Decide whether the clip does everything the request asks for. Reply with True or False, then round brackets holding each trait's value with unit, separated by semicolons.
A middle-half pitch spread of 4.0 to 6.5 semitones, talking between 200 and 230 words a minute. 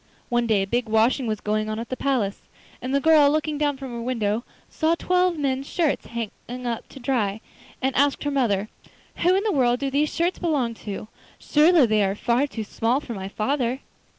True (4.6 semitones; 205 wpm)